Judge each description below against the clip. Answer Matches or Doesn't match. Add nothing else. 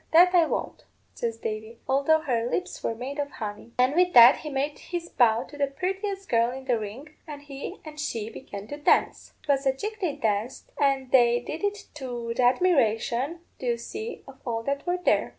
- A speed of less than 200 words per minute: Doesn't match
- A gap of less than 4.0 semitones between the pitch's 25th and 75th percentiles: Doesn't match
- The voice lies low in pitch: Doesn't match